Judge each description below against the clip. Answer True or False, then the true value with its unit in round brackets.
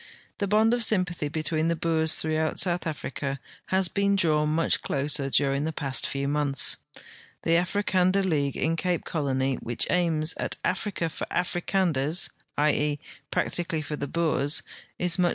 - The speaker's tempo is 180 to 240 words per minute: False (160 wpm)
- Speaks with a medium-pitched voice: True (160 Hz)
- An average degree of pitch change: True (3.5 semitones)